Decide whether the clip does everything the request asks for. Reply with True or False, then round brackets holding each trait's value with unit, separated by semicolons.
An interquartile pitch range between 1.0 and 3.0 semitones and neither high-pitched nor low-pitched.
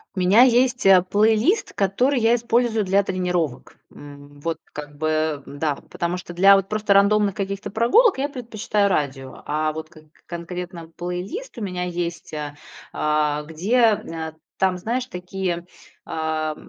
False (5.3 semitones; 180 Hz)